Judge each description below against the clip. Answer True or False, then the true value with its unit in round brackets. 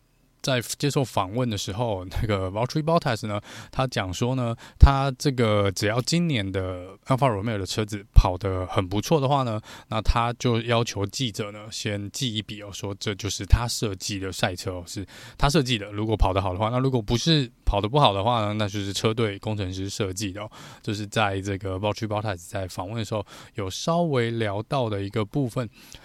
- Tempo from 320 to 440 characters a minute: True (350 characters per minute)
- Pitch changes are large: False (4.0 semitones)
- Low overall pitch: True (110 Hz)